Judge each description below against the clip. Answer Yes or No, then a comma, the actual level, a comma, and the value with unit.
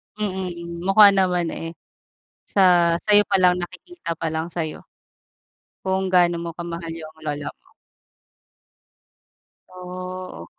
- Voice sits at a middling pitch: Yes, medium, 180 Hz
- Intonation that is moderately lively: No, narrow, 2.0 semitones